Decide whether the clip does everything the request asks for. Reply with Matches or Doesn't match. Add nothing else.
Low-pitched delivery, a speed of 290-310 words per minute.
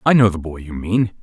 Matches